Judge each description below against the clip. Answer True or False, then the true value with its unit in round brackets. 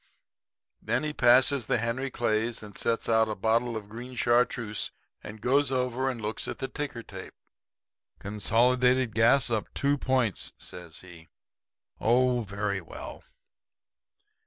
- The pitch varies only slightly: False (3.0 semitones)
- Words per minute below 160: True (135 wpm)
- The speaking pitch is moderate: False (115 Hz)